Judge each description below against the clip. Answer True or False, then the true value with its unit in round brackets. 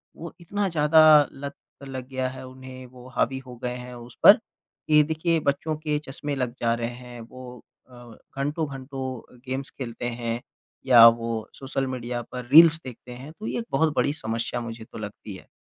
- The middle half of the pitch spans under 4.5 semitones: True (3.3 semitones)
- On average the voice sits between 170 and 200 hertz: False (130 Hz)